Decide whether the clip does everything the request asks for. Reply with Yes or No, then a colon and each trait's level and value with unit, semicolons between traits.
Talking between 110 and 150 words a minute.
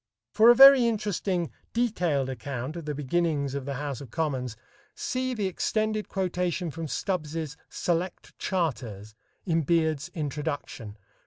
Yes: average, 140 wpm